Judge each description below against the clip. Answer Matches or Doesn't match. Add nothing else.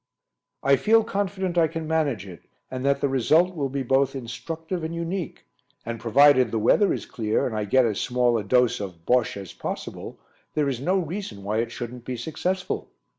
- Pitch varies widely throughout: Matches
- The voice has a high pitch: Doesn't match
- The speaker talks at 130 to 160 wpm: Doesn't match